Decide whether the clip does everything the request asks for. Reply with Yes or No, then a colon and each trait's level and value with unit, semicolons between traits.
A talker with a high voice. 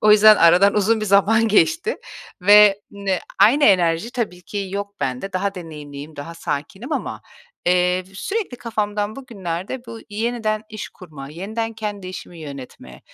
Yes: high, 200 Hz